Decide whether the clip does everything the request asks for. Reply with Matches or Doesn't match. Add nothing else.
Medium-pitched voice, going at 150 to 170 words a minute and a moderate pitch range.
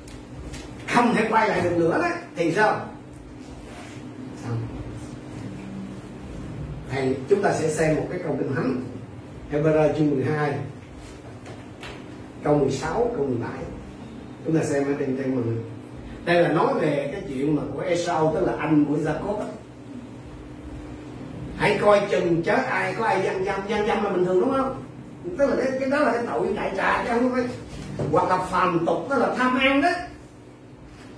Doesn't match